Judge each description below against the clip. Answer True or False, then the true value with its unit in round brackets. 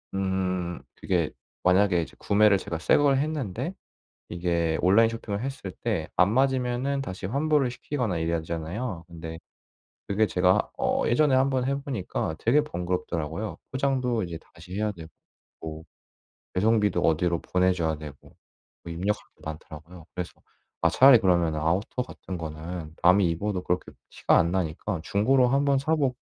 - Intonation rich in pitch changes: True (6.7 semitones)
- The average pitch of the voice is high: False (95 Hz)